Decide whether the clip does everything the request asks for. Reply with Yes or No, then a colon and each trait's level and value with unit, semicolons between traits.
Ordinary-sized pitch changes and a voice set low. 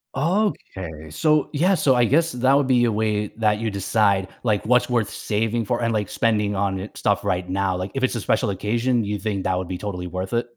Yes: average, 4.1 semitones; low, 110 Hz